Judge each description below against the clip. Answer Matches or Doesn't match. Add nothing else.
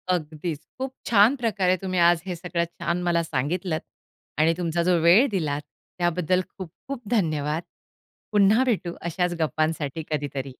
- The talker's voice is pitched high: Doesn't match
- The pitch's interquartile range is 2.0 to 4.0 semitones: Matches